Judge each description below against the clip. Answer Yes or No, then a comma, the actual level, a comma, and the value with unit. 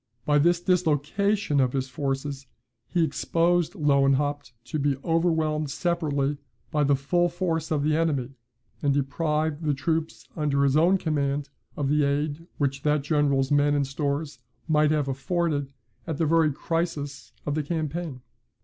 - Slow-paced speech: No, average, 150 wpm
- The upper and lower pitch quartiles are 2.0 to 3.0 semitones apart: Yes, narrow, 2.6 semitones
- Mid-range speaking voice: Yes, medium, 150 Hz